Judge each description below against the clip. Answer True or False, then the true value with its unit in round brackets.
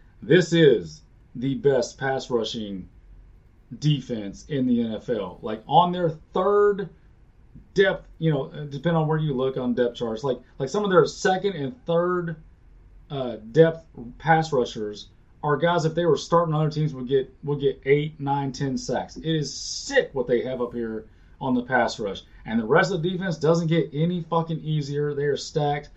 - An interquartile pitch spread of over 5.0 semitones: True (5.4 semitones)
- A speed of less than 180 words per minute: False (185 wpm)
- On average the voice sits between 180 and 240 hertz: False (145 Hz)